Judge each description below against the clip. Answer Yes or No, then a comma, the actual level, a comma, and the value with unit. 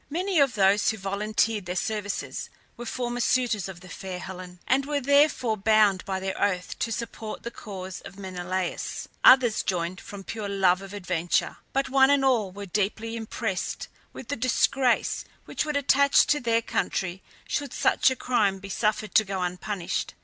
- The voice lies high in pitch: Yes, high, 210 Hz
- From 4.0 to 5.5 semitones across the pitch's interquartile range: Yes, average, 4.4 semitones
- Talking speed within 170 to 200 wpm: Yes, average, 175 wpm